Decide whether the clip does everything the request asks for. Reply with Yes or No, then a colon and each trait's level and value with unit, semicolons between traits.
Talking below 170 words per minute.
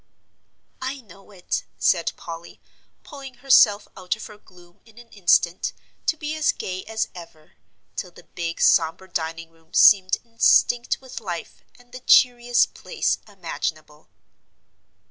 Yes: average, 140 wpm